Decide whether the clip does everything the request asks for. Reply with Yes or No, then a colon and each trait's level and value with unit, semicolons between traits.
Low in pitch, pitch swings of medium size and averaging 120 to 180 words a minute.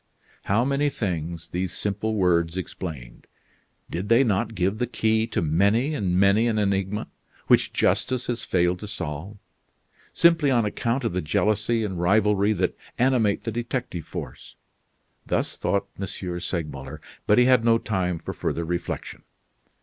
Yes: low, 100 Hz; average, 4.5 semitones; average, 150 wpm